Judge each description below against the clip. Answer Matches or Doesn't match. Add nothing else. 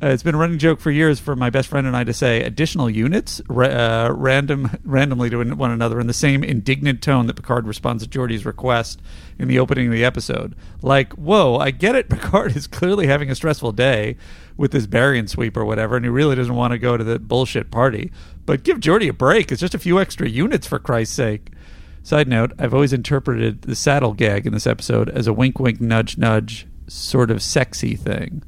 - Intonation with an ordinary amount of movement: Matches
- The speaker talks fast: Matches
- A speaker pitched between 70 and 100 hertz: Doesn't match